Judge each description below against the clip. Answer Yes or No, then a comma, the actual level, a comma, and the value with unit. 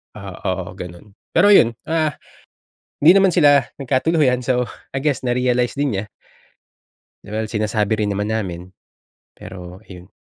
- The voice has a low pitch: Yes, low, 115 Hz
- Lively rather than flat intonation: Yes, wide, 6.0 semitones